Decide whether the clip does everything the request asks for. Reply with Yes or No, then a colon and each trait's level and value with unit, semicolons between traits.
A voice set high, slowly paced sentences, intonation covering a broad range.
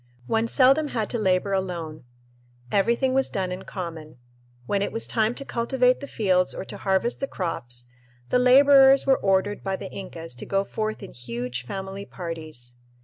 No: high, 195 Hz; average, 175 wpm; wide, 5.9 semitones